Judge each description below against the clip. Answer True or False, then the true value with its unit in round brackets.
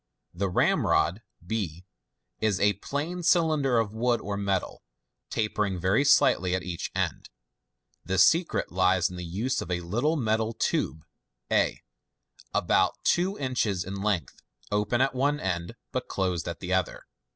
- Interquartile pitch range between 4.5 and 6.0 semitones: True (5.4 semitones)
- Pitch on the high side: False (100 Hz)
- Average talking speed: True (150 wpm)